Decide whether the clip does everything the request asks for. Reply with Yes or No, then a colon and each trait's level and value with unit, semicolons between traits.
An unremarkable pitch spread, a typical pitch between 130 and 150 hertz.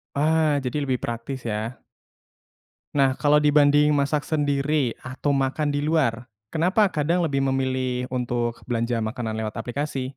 Yes: average, 3.3 semitones; low, 135 Hz